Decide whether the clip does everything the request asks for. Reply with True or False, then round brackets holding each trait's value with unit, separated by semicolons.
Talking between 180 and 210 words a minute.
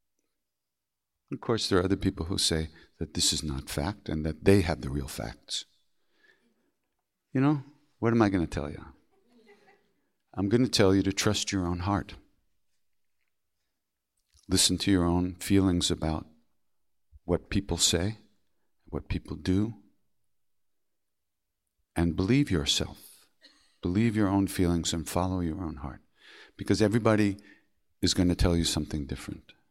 False (145 wpm)